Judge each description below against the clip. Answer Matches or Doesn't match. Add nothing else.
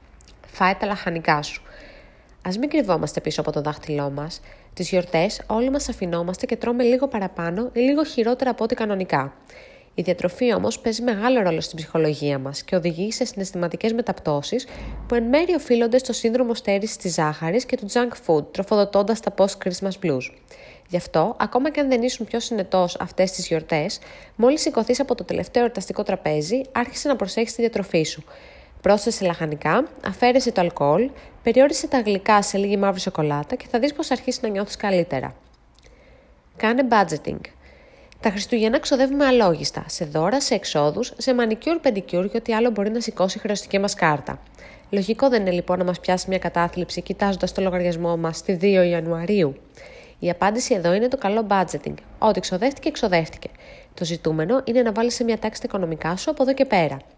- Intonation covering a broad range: Matches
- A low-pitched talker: Doesn't match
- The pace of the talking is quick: Matches